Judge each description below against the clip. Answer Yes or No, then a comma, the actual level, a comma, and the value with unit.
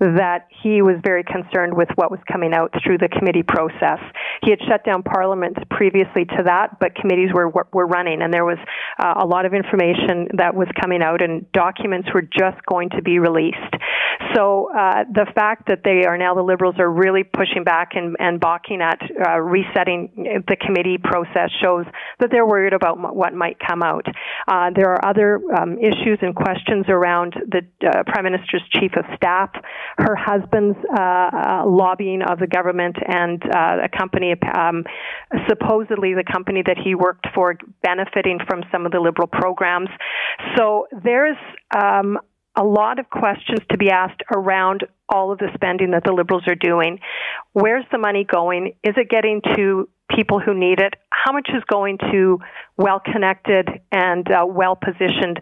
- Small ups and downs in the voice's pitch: Yes, narrow, 2.2 semitones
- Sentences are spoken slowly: No, average, 180 wpm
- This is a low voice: No, medium, 185 Hz